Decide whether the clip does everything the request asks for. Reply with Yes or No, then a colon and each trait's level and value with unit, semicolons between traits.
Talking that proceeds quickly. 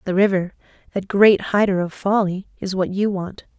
No: average, 185 wpm